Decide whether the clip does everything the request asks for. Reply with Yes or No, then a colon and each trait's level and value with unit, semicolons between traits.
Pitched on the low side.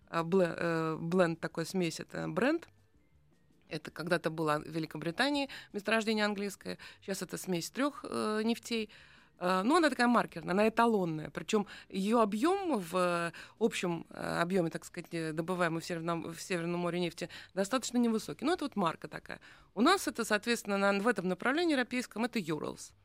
No: medium, 185 Hz